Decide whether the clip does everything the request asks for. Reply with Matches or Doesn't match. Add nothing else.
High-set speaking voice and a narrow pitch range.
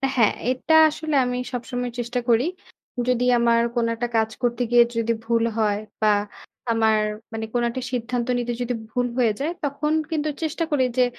Matches